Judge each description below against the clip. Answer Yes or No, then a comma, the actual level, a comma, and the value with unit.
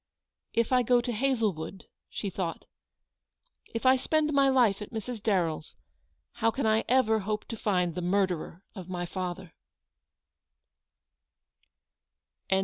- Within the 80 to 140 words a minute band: Yes, slow, 135 wpm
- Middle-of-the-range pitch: No, high, 215 Hz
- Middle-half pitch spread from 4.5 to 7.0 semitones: Yes, average, 4.9 semitones